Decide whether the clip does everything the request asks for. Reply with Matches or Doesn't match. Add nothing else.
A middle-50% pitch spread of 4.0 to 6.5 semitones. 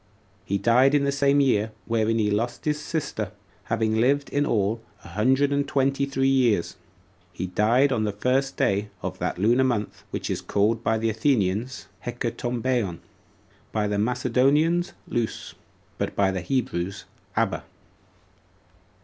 Matches